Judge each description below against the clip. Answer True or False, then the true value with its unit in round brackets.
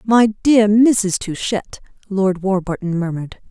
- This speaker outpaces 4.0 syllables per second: False (3.9 syllables/s)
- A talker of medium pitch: False (200 Hz)